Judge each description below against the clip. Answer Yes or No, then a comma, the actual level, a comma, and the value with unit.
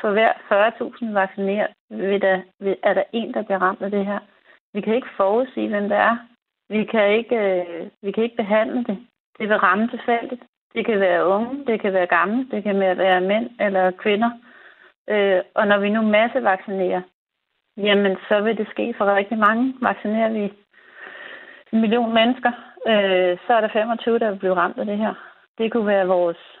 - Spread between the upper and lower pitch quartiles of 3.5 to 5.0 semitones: No, average, 2.7 semitones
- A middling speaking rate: Yes, average, 180 wpm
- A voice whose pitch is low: No, high, 210 Hz